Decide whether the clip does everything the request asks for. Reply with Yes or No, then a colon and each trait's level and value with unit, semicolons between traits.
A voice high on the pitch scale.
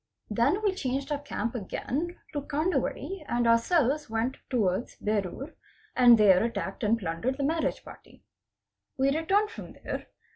Yes: very high, 260 Hz